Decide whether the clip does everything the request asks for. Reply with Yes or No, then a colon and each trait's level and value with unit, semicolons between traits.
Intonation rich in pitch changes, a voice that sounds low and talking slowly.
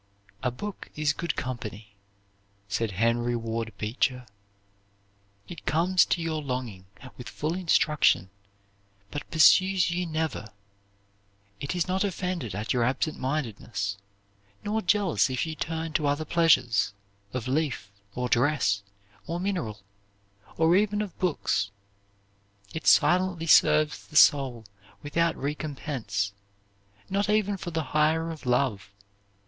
No: wide, 6.1 semitones; medium, 150 Hz; slow, 125 wpm